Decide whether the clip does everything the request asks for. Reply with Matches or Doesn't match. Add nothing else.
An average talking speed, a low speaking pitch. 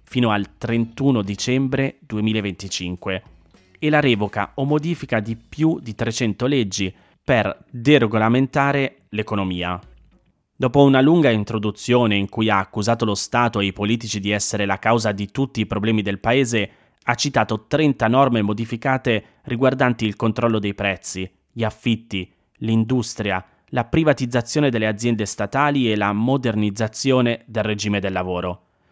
Matches